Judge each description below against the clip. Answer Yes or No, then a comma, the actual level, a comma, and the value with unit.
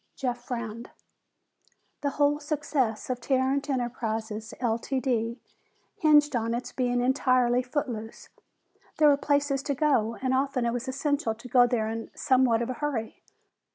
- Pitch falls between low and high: No, very high, 255 Hz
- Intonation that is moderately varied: Yes, average, 3.2 semitones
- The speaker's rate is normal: Yes, average, 145 wpm